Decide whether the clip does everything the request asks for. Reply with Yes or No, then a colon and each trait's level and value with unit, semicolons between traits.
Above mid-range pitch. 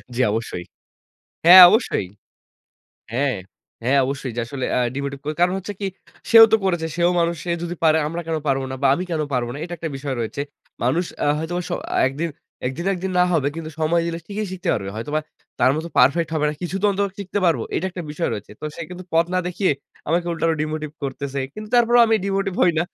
No: medium, 165 Hz